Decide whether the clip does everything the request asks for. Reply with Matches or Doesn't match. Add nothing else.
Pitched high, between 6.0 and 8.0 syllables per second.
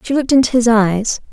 Matches